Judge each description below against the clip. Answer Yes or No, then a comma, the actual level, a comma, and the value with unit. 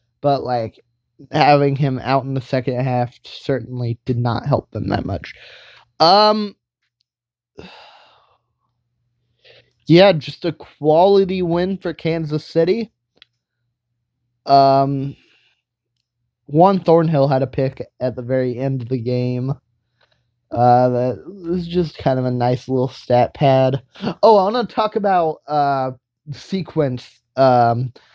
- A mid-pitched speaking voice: No, low, 130 Hz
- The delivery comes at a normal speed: No, slow, 125 wpm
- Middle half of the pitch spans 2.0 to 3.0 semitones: No, average, 4.0 semitones